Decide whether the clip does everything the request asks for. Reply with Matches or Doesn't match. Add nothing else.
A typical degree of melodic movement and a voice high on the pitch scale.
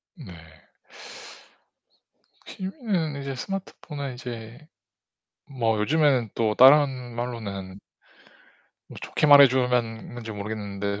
Doesn't match